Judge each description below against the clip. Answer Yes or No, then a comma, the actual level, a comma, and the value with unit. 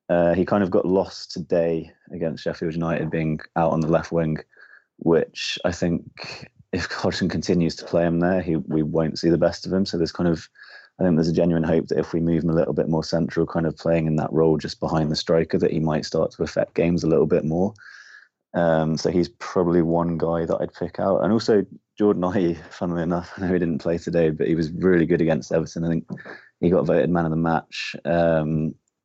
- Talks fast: Yes, fast, 235 wpm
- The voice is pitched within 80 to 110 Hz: Yes, very low, 85 Hz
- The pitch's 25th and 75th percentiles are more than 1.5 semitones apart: No, narrow, 1.2 semitones